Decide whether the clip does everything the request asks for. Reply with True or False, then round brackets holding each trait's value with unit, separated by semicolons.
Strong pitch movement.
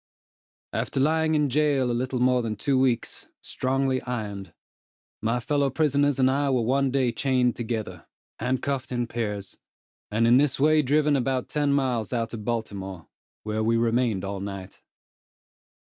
False (3.5 semitones)